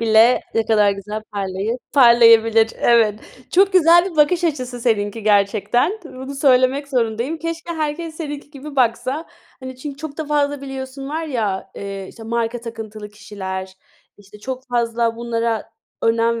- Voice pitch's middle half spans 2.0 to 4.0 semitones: No, average, 4.5 semitones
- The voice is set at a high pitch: Yes, high, 240 Hz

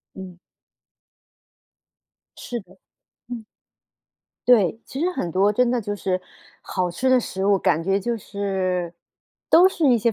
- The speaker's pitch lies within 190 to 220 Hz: Yes, high, 200 Hz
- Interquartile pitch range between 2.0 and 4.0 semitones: No, average, 4.7 semitones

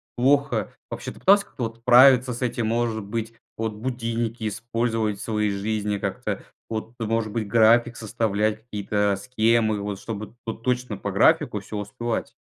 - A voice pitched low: Yes, low, 115 Hz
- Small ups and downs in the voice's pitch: Yes, narrow, 2.0 semitones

